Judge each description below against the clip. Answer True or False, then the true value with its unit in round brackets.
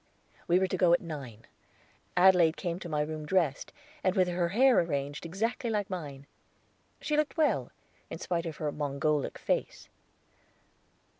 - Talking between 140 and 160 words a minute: True (155 wpm)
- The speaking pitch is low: False (170 Hz)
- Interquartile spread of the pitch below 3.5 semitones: False (4.0 semitones)